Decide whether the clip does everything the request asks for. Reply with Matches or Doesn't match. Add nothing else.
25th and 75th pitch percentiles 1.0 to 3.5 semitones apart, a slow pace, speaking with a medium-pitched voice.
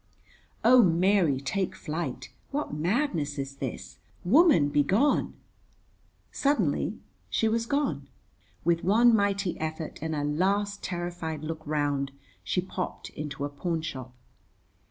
Doesn't match